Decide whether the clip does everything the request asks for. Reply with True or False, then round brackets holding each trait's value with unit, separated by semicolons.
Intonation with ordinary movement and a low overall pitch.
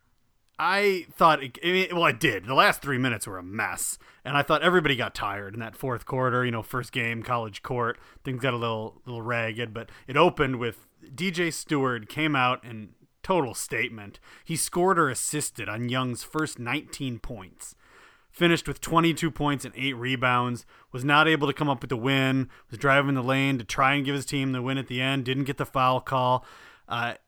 True (3.3 semitones; 130 Hz)